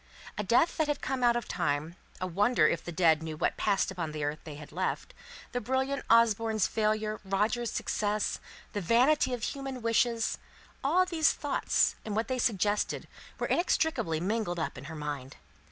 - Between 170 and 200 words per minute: Yes, average, 180 wpm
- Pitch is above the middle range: Yes, high, 215 Hz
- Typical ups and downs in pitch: No, wide, 6.5 semitones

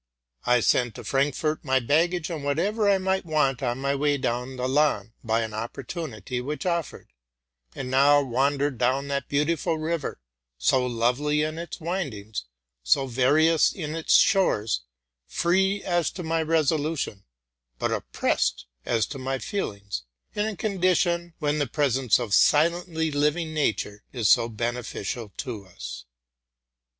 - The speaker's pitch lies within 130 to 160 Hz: Yes, medium, 140 Hz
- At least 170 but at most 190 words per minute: No, average, 145 wpm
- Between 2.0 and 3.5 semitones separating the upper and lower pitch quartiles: No, average, 5.1 semitones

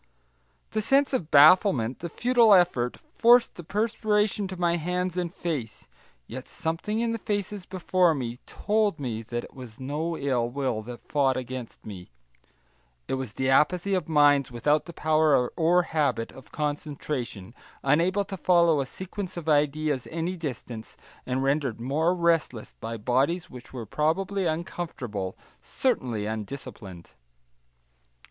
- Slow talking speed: No, average, 145 wpm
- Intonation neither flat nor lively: No, wide, 6.0 semitones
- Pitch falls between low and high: Yes, medium, 150 Hz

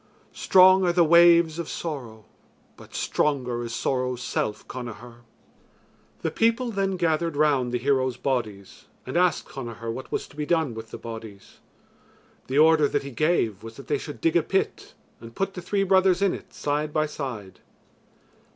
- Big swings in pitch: Yes, wide, 6.3 semitones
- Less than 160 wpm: No, average, 170 wpm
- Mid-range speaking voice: Yes, medium, 145 Hz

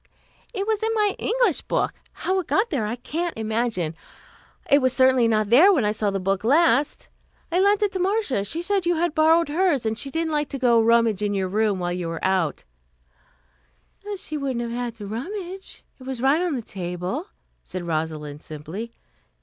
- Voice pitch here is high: Yes, very high, 250 Hz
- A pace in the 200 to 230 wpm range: Yes, fast, 205 wpm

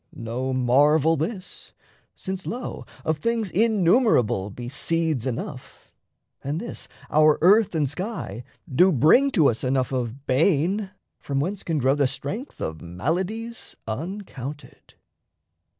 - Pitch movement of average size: No, wide, 6.8 semitones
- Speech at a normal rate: No, slow, 125 wpm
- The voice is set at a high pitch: No, medium, 155 Hz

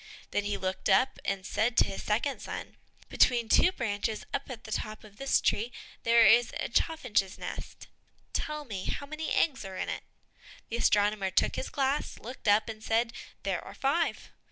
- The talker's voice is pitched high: Yes, high, 230 Hz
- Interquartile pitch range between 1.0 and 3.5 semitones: No, average, 4.5 semitones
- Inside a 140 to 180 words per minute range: No, average, 190 wpm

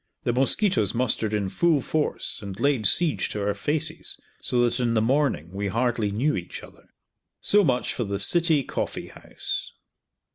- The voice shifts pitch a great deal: Yes, wide, 6.3 semitones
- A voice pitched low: Yes, low, 120 Hz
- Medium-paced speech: Yes, average, 170 wpm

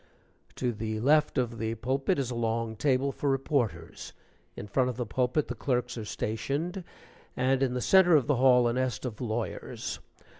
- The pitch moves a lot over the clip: No, average, 3.0 semitones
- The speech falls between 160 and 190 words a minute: Yes, average, 185 wpm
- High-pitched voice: No, low, 125 Hz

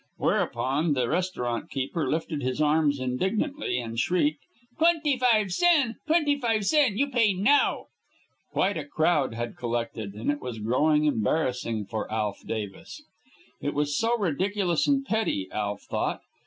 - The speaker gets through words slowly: No, average, 145 wpm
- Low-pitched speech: No, medium, 155 Hz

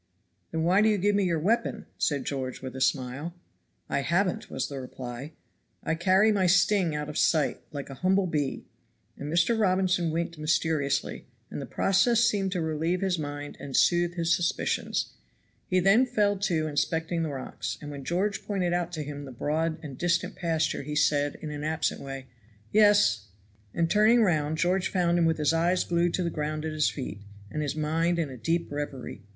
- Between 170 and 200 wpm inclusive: Yes, average, 195 wpm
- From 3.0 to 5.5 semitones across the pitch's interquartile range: Yes, average, 3.8 semitones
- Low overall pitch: No, medium, 165 Hz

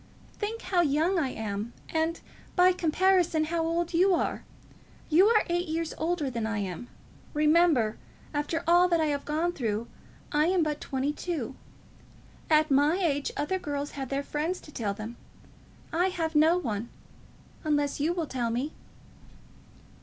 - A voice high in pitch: Yes, very high, 310 Hz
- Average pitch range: Yes, average, 3.9 semitones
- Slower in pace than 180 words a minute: Yes, average, 160 wpm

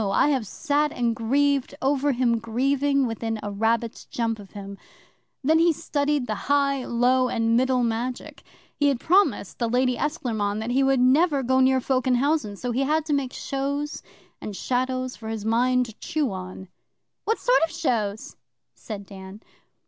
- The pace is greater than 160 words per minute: Yes, average, 170 wpm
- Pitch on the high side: Yes, very high, 255 Hz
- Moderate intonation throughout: Yes, average, 3.9 semitones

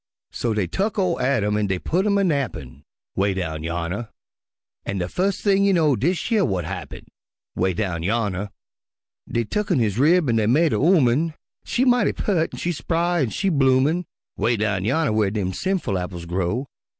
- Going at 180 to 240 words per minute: Yes, average, 185 wpm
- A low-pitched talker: Yes, low, 120 Hz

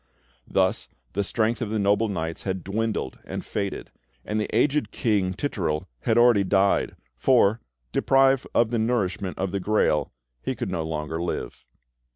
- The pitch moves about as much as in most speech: Yes, average, 3.6 semitones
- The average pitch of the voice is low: Yes, low, 100 Hz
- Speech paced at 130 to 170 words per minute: Yes, average, 160 wpm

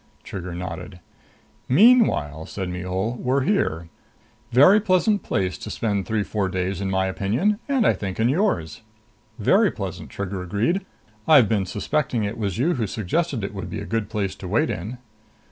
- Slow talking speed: No, average, 170 wpm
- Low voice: Yes, low, 105 Hz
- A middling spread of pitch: No, wide, 7.4 semitones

